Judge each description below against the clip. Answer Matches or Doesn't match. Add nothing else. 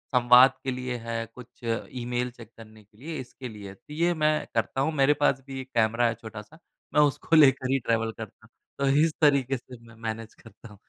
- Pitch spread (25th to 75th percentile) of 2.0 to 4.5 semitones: Matches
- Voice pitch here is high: Doesn't match